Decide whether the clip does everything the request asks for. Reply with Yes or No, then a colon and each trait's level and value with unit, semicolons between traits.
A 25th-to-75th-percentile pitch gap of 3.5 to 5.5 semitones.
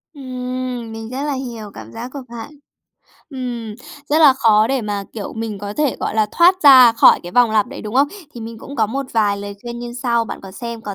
No: average, 2.9 semitones